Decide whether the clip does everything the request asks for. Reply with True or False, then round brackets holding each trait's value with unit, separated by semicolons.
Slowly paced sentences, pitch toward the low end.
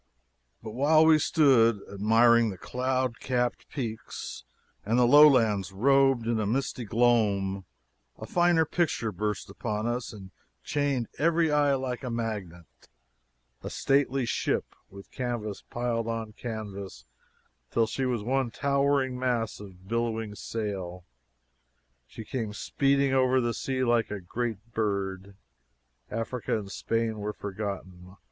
True (130 wpm; 115 Hz)